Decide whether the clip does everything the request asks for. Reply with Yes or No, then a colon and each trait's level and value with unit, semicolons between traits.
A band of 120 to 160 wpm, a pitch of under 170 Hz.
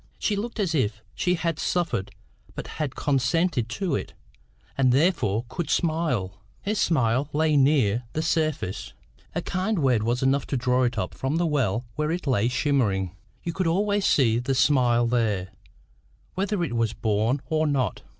No: average, 170 wpm; low, 135 Hz